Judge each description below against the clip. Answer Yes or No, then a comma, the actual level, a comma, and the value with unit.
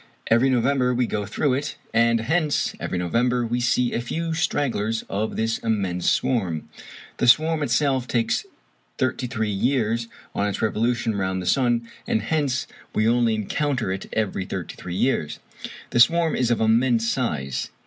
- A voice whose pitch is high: No, low, 115 Hz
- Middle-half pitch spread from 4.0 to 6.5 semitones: No, average, 3.2 semitones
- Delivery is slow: No, average, 160 wpm